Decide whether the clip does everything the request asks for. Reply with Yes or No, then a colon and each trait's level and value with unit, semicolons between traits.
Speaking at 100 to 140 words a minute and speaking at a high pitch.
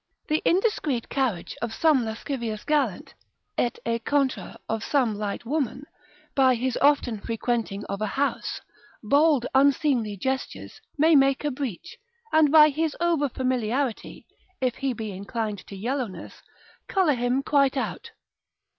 Yes: slow, 135 wpm; very high, 260 Hz